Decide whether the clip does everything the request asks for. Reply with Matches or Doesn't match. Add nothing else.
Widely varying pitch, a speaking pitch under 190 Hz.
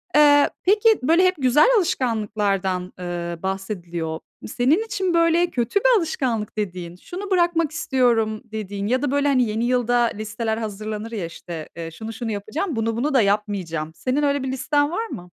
Doesn't match